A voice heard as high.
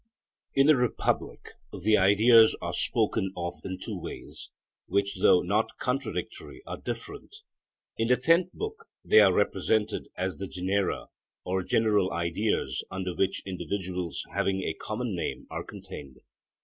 No: low, 100 Hz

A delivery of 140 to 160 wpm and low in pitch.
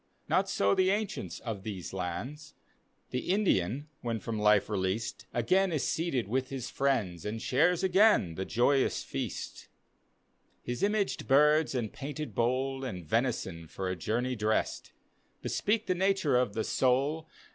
Yes: average, 150 wpm; low, 125 Hz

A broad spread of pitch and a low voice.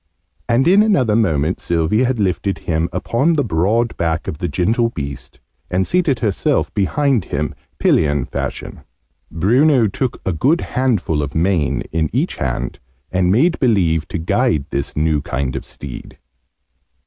Yes: wide, 7.3 semitones; very low, 95 Hz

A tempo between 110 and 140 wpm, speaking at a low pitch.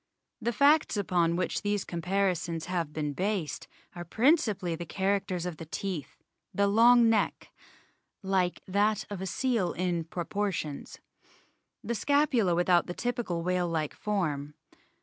No: slow, 135 wpm; medium, 185 Hz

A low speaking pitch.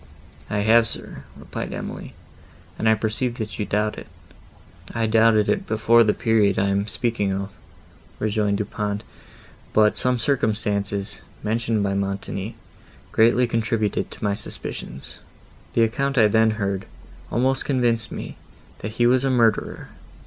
Yes: low, 110 Hz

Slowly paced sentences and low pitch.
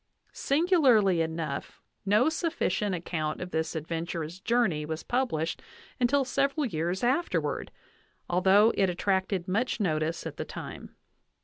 No: slow, 125 wpm; high, 190 Hz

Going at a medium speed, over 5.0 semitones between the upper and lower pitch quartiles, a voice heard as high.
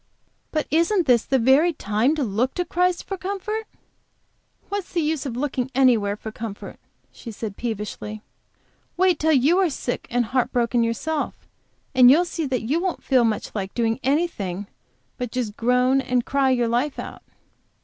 Yes: average, 170 wpm; wide, 5.6 semitones; very high, 255 Hz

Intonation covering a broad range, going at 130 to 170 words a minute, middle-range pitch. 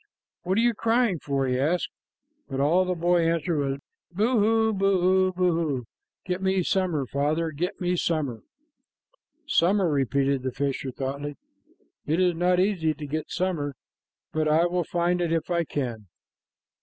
No: average, 4.3 semitones; average, 155 wpm; medium, 170 Hz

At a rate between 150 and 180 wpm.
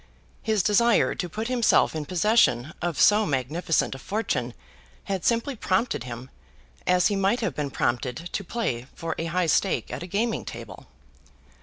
Yes: average, 165 wpm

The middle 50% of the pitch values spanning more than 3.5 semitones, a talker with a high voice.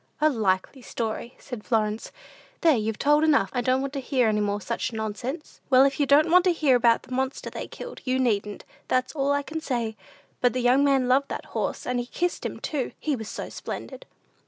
Yes: average, 3.9 semitones; very high, 255 Hz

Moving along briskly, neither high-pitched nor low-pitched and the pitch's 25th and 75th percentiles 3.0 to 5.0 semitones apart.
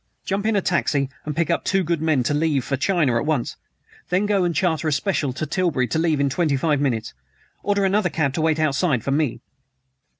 Yes: fast, 225 wpm; medium, 155 Hz; average, 4.2 semitones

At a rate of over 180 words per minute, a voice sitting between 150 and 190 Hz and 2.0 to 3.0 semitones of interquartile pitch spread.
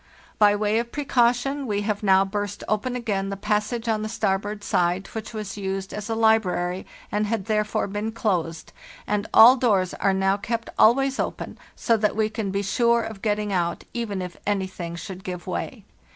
No: average, 190 wpm; high, 210 Hz; narrow, 2.6 semitones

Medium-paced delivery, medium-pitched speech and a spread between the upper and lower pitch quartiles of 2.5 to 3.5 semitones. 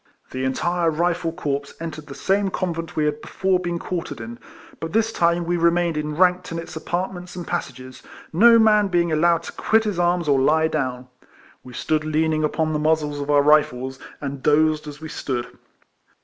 Yes: average, 185 wpm; medium, 160 Hz; average, 2.9 semitones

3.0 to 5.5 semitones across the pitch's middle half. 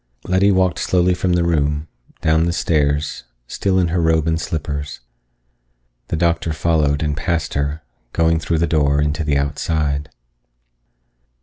No: narrow, 2.5 semitones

